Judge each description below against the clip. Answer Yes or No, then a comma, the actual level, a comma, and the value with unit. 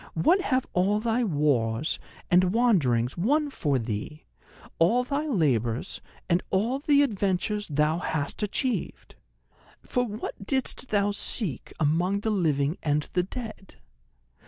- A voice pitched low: No, high, 190 Hz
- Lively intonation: Yes, wide, 7.6 semitones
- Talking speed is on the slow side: Yes, slow, 130 wpm